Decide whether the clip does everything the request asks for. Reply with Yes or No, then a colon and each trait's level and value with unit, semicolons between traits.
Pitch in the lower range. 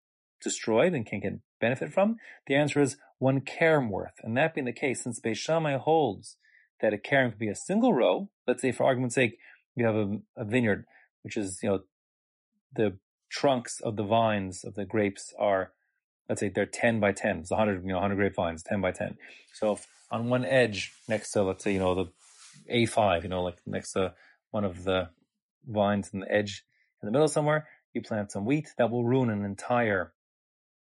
Yes: low, 115 Hz